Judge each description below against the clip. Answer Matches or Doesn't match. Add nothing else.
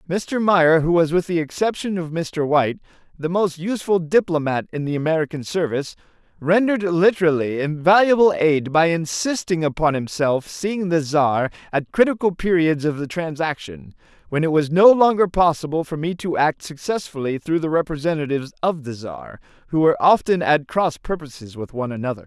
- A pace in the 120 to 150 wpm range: Doesn't match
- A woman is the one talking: Doesn't match